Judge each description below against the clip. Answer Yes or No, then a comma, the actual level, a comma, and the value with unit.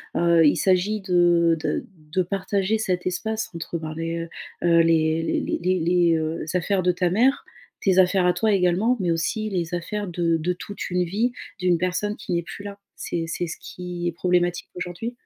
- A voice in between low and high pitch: Yes, medium, 180 Hz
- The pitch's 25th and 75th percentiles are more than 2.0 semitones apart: Yes, narrow, 2.5 semitones